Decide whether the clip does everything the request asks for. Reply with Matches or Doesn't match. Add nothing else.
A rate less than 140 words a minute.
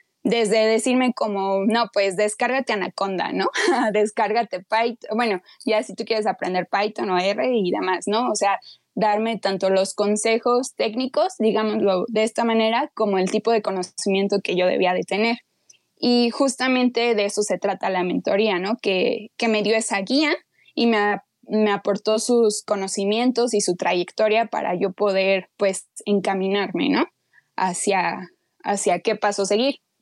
Doesn't match